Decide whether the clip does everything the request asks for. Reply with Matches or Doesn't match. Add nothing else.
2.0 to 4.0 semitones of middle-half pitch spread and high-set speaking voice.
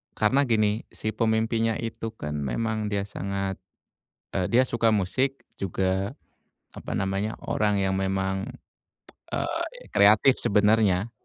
Doesn't match